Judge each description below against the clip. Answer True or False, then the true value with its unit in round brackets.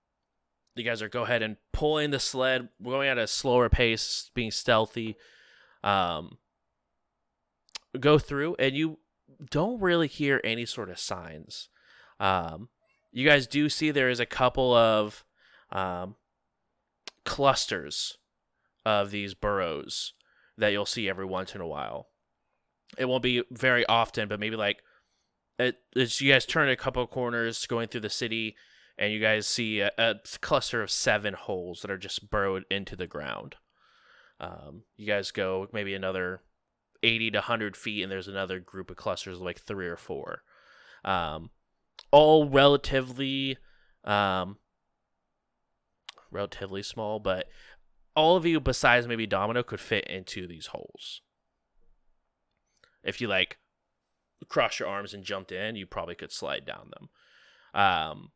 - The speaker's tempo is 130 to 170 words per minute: True (150 wpm)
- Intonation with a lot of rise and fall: False (4.8 semitones)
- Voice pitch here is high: False (110 Hz)